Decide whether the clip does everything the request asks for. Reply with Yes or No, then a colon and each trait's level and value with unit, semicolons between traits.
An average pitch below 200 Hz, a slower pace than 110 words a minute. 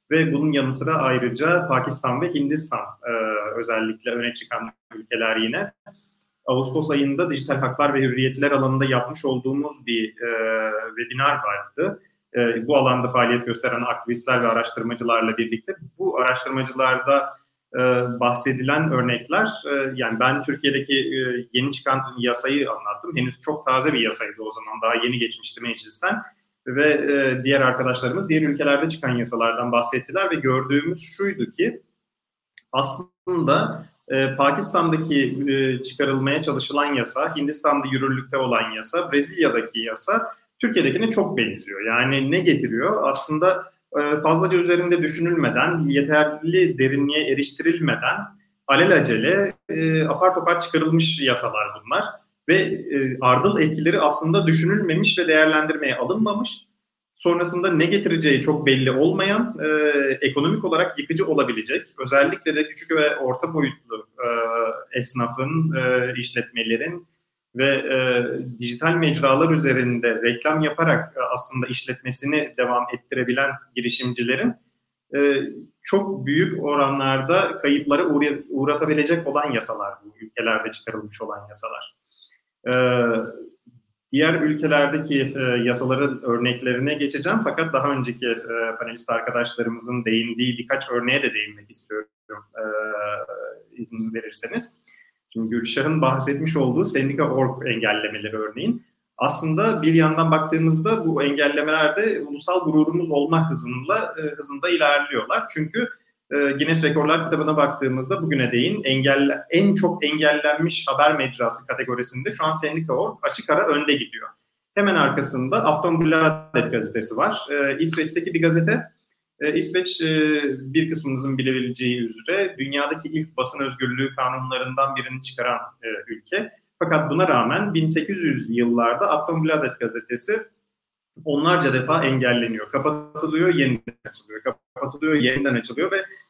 No: medium, 140 Hz; average, 120 wpm